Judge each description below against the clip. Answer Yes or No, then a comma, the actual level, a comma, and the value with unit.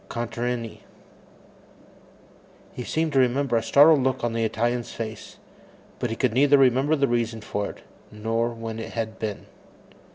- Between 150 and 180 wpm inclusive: Yes, average, 155 wpm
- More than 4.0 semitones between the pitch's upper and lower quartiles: No, narrow, 2.6 semitones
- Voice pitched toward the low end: Yes, low, 120 Hz